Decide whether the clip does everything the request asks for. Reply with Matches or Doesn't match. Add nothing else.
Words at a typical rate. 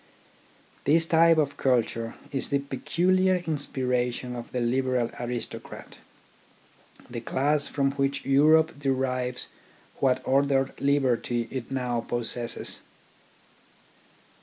Doesn't match